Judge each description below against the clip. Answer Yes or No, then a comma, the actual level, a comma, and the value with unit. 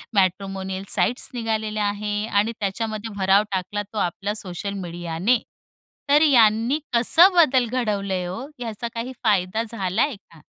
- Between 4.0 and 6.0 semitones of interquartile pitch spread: No, average, 3.3 semitones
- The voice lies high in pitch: Yes, high, 210 Hz